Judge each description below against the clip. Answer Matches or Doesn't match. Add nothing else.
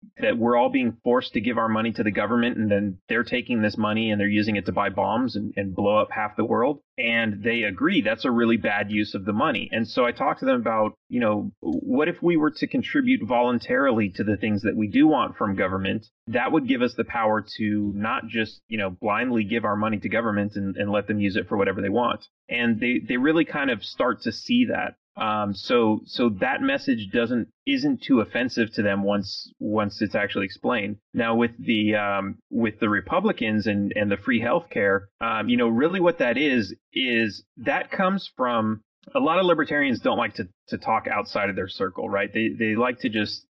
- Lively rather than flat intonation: Matches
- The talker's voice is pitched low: Matches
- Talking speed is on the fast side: Matches